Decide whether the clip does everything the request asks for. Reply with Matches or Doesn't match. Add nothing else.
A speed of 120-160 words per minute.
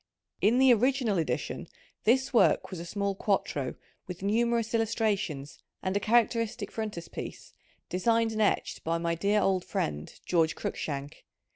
Matches